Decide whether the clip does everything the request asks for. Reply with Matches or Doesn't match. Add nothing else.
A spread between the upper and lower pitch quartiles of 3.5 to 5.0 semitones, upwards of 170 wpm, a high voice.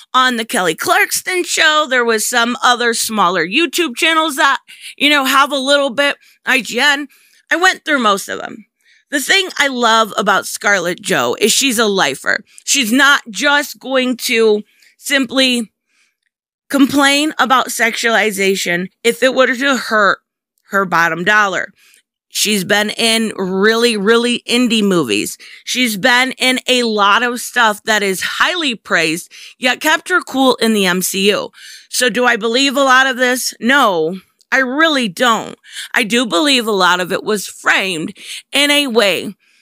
Doesn't match